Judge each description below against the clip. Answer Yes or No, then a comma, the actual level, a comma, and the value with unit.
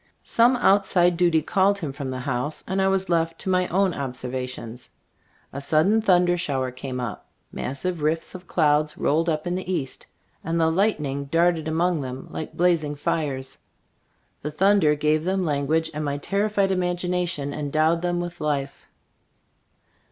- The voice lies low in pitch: No, medium, 160 Hz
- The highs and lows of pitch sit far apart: No, average, 4.0 semitones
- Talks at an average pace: Yes, average, 160 wpm